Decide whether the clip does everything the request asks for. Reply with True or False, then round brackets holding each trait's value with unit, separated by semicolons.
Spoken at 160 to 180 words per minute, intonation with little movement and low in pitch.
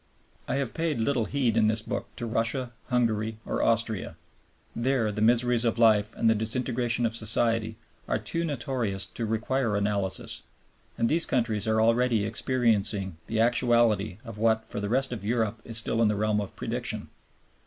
True (175 wpm; 2.1 semitones; 115 Hz)